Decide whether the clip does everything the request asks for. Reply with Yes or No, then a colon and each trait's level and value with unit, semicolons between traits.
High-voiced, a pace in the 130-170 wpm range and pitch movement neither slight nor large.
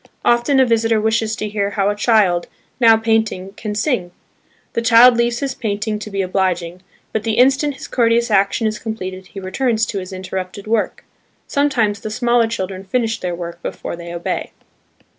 No: high, 215 Hz; average, 180 wpm; average, 3.4 semitones